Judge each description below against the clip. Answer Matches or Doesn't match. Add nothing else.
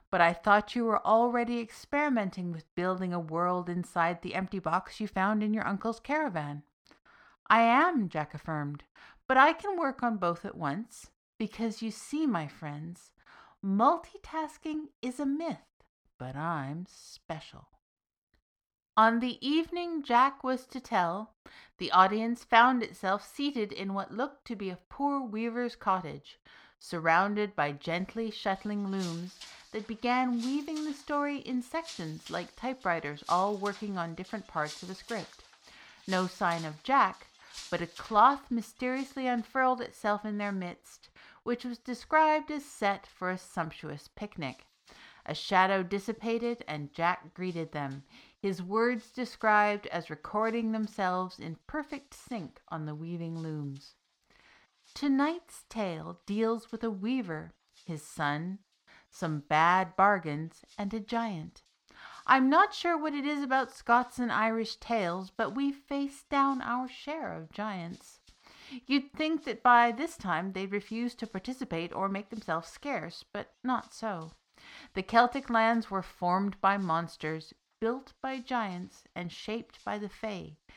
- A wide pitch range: Matches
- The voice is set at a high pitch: Matches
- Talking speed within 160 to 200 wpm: Doesn't match